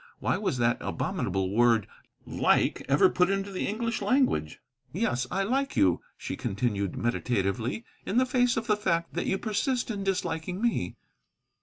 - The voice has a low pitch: No, medium, 185 Hz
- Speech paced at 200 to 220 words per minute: No, average, 160 wpm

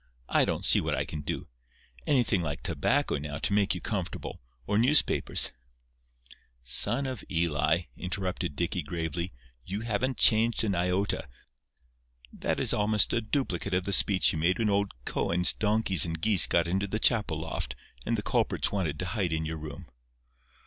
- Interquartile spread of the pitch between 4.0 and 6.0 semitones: Yes, average, 4.5 semitones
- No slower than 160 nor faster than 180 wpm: Yes, average, 165 wpm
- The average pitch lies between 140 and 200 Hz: No, very low, 90 Hz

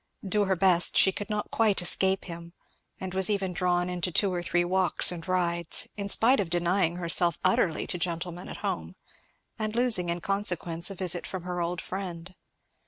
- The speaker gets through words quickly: No, average, 185 wpm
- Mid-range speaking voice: Yes, medium, 180 Hz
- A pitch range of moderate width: No, narrow, 2.0 semitones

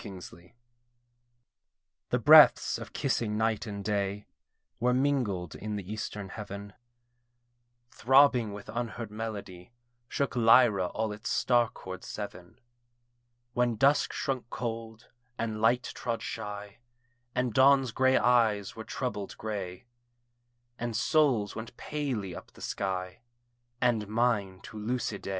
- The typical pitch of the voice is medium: No, low, 110 Hz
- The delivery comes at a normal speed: No, slow, 125 wpm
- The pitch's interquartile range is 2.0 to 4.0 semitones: Yes, average, 3.2 semitones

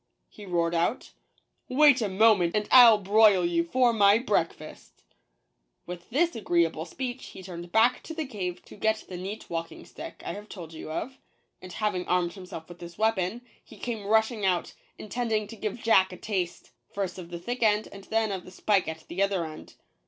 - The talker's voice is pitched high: Yes, high, 200 Hz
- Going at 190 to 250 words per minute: Yes, fast, 205 wpm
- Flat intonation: No, average, 4.1 semitones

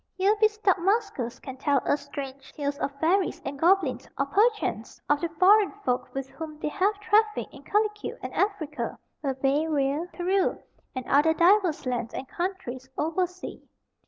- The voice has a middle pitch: No, very high, 320 Hz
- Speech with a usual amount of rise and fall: No, wide, 6.2 semitones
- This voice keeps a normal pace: Yes, average, 160 wpm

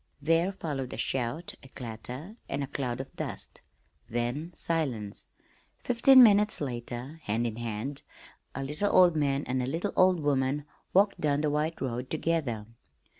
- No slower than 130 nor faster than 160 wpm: Yes, average, 155 wpm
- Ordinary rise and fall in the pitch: Yes, average, 4.9 semitones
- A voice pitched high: No, medium, 140 Hz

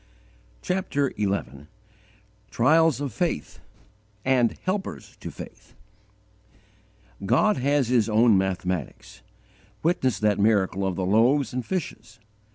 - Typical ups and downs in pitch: No, wide, 6.5 semitones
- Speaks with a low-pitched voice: Yes, low, 115 Hz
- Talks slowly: Yes, slow, 105 wpm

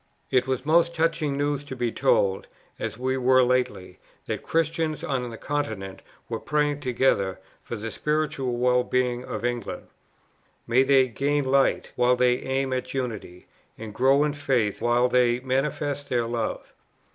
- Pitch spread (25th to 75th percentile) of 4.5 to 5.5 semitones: No, average, 2.9 semitones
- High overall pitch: No, low, 130 Hz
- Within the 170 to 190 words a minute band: No, average, 160 wpm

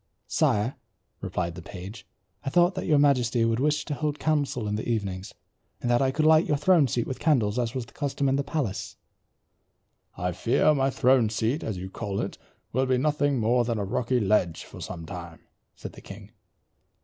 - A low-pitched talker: Yes, low, 120 Hz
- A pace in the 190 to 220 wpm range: Yes, average, 200 wpm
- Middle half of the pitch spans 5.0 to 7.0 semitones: Yes, wide, 5.5 semitones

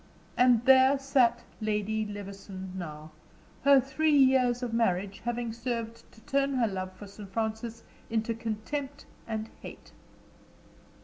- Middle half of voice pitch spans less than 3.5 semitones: No, average, 3.9 semitones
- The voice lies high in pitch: Yes, high, 230 Hz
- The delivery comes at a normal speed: No, slow, 130 wpm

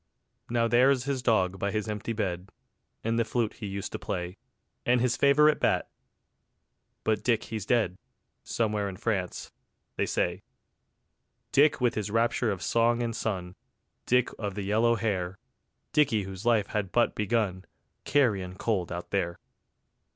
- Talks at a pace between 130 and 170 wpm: Yes, average, 150 wpm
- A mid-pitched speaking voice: No, low, 110 Hz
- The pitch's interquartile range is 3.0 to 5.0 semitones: Yes, average, 3.5 semitones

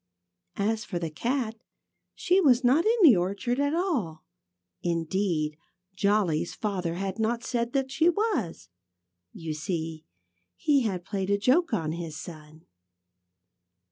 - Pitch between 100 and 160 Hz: No, high, 200 Hz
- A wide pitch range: Yes, wide, 7.6 semitones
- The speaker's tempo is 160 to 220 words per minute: No, slow, 135 wpm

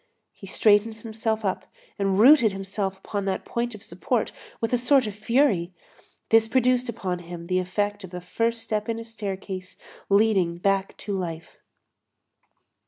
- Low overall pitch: No, high, 205 Hz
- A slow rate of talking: No, average, 160 wpm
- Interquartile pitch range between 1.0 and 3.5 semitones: Yes, average, 3.1 semitones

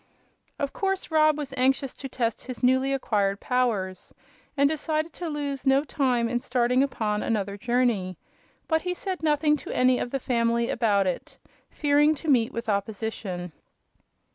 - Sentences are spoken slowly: No, average, 160 wpm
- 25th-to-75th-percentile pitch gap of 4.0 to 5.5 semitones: Yes, average, 4.3 semitones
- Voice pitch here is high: Yes, very high, 255 Hz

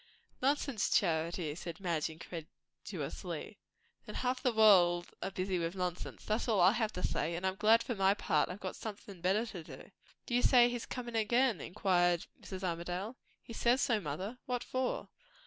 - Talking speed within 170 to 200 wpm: Yes, average, 175 wpm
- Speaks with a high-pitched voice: Yes, high, 195 Hz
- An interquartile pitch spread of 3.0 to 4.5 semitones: No, average, 5.0 semitones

